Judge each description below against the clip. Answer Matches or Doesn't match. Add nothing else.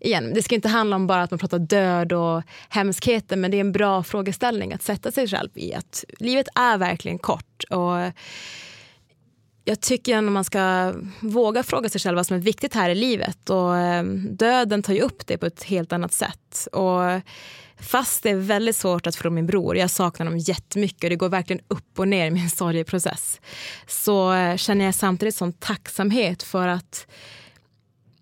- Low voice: Doesn't match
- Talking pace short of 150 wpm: Doesn't match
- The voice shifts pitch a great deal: Doesn't match